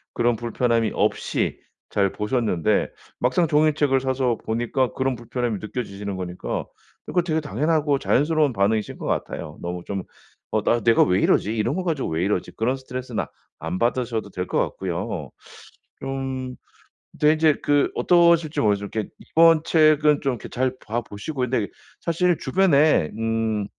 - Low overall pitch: Yes, low, 125 Hz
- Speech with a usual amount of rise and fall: No, wide, 5.8 semitones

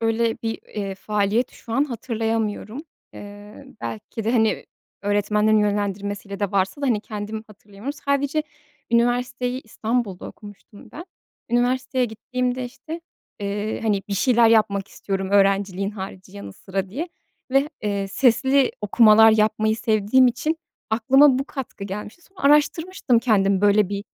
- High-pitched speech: Yes, high, 220 Hz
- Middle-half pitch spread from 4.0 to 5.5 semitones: No, average, 3.5 semitones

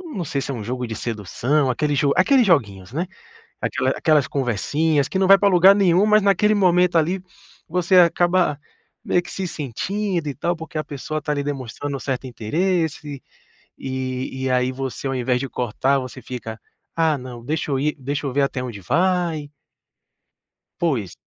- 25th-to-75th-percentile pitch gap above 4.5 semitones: Yes, average, 5.3 semitones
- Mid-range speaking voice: Yes, medium, 145 Hz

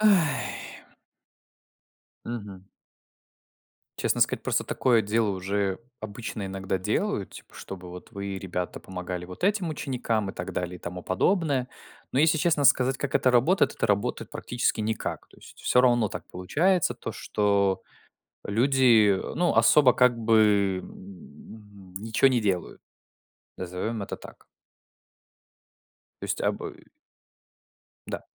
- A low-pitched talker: Yes, low, 110 Hz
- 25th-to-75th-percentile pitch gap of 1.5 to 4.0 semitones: No, average, 4.9 semitones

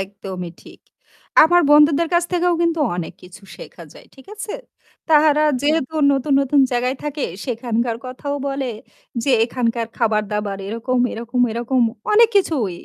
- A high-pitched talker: Yes, very high, 255 Hz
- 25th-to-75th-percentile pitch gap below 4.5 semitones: No, average, 4.9 semitones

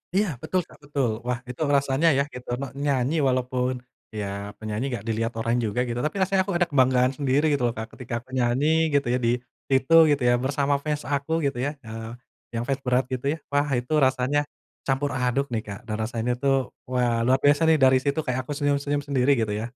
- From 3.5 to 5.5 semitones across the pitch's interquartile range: No, average, 2.7 semitones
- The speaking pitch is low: Yes, low, 130 Hz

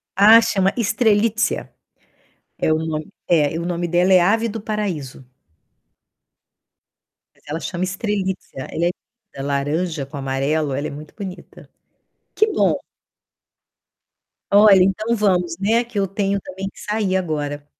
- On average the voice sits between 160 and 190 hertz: Yes, medium, 185 Hz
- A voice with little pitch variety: No, average, 4.8 semitones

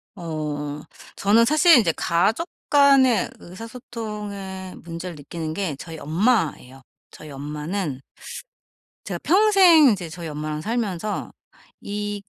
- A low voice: No, high, 190 Hz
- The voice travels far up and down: Yes, wide, 6.7 semitones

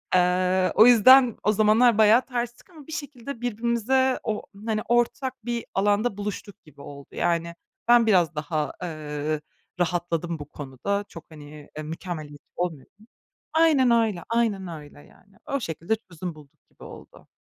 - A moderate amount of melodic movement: No, wide, 6.3 semitones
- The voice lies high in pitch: Yes, high, 200 Hz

